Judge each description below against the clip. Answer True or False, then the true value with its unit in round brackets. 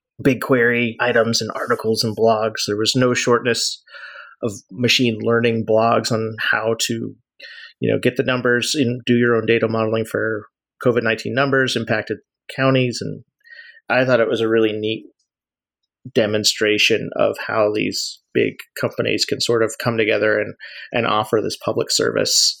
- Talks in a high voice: False (115 Hz)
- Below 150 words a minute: False (155 wpm)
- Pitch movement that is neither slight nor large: False (2.2 semitones)